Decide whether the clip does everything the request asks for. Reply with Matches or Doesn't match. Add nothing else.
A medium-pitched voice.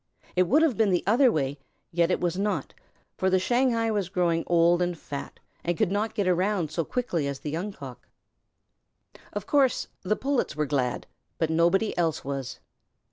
Matches